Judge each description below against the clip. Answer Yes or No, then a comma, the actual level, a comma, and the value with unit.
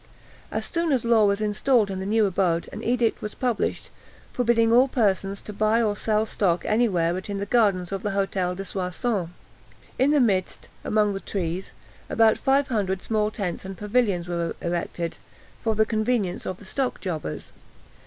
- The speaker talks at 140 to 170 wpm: No, average, 185 wpm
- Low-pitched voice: No, high, 205 Hz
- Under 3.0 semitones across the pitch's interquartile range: No, average, 3.4 semitones